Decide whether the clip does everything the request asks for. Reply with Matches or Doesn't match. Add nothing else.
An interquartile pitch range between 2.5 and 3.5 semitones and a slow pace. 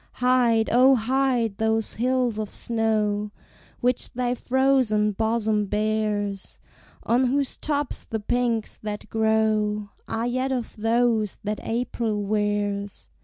Matches